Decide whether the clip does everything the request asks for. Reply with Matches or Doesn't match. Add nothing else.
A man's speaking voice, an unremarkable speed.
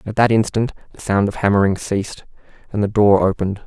Matches